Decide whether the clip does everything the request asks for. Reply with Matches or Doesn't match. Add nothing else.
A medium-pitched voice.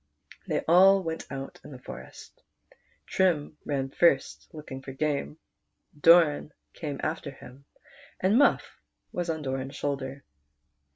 Matches